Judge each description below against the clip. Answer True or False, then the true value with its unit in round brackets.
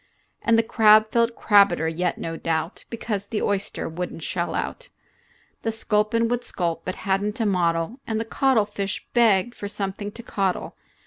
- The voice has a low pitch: False (205 Hz)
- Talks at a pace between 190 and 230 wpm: False (175 wpm)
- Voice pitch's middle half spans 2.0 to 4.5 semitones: True (3.9 semitones)